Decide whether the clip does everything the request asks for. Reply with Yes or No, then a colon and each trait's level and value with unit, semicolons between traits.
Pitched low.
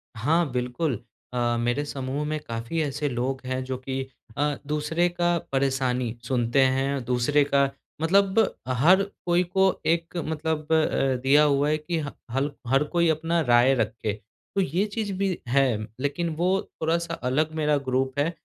No: medium, 145 Hz